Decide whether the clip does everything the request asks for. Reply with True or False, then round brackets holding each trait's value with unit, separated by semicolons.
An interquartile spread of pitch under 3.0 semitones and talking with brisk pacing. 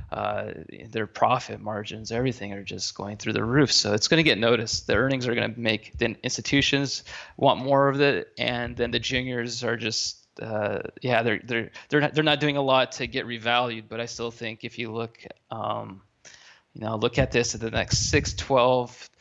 True (2.4 semitones; 210 wpm)